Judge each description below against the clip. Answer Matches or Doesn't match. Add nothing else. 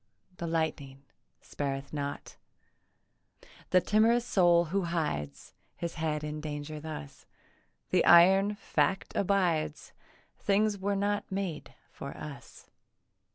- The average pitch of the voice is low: Doesn't match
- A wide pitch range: Doesn't match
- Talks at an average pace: Doesn't match